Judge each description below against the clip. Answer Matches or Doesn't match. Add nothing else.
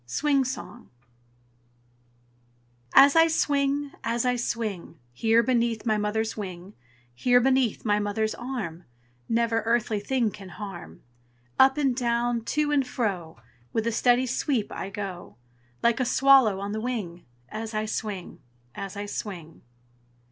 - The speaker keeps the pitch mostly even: Doesn't match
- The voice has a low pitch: Doesn't match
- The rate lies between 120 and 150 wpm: Matches